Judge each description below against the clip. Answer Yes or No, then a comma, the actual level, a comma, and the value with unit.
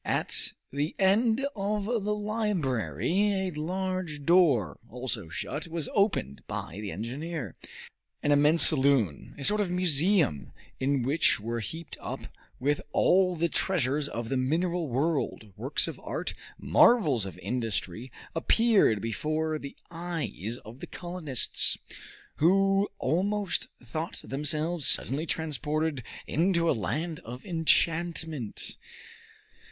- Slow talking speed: Yes, slow, 120 wpm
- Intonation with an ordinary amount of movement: No, wide, 6.0 semitones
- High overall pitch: No, medium, 155 Hz